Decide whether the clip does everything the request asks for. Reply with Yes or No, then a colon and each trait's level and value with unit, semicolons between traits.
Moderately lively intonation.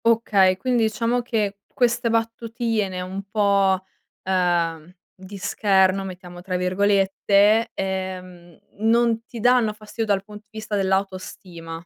Yes: average, 3.2 semitones